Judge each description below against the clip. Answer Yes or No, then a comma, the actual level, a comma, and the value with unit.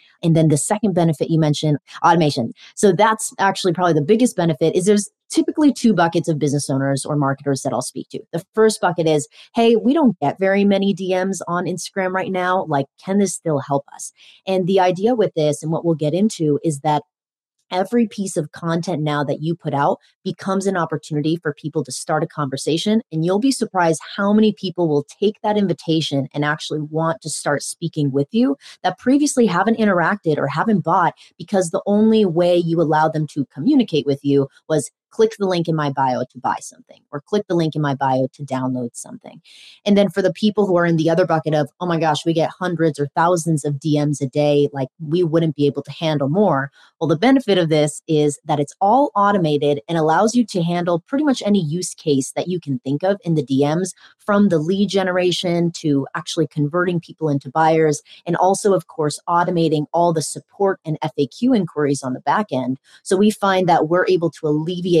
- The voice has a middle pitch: Yes, medium, 165 Hz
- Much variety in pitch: No, average, 4.5 semitones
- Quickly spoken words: Yes, fast, 210 wpm